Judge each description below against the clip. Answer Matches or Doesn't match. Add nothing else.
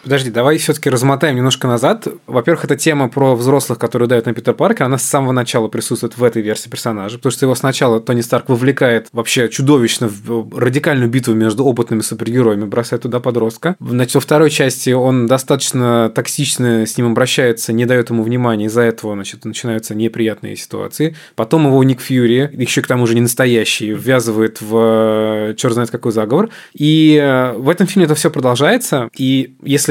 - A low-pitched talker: Matches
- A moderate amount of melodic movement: Matches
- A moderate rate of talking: Doesn't match